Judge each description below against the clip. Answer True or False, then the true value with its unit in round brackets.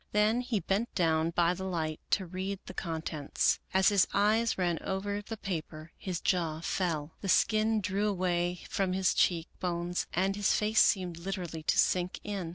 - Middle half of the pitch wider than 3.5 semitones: False (3.0 semitones)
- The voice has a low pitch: False (185 Hz)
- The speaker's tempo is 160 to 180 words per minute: True (175 wpm)